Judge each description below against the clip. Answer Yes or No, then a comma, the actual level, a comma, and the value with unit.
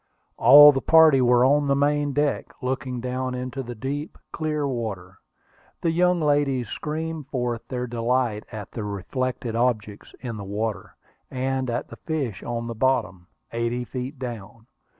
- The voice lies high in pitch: No, low, 125 Hz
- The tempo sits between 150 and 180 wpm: Yes, average, 155 wpm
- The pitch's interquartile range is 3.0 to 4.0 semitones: Yes, average, 3.4 semitones